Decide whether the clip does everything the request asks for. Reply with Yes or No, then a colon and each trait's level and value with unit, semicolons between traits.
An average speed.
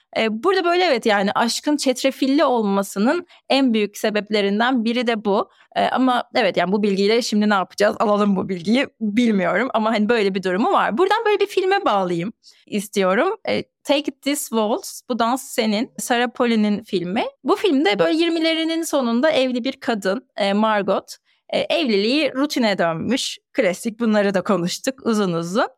No: fast, 150 wpm